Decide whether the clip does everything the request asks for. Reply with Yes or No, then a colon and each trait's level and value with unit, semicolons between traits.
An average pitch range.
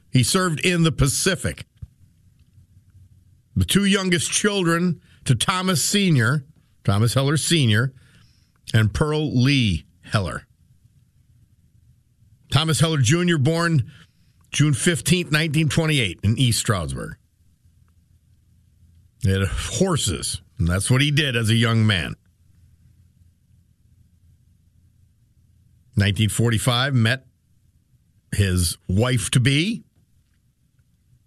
No: wide, 6.6 semitones